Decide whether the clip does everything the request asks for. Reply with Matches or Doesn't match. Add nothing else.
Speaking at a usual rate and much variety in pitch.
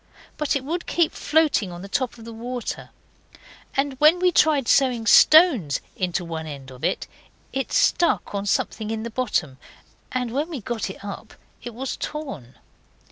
Matches